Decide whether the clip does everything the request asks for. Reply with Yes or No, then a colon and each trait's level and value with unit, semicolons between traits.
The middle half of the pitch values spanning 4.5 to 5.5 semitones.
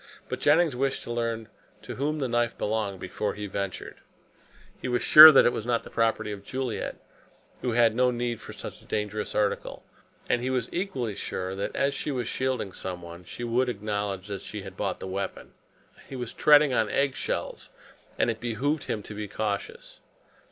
No: average, 3.9 semitones